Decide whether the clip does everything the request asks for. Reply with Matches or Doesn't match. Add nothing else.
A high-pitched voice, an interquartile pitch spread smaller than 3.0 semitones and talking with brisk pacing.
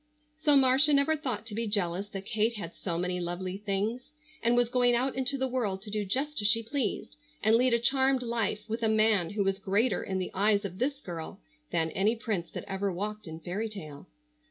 Doesn't match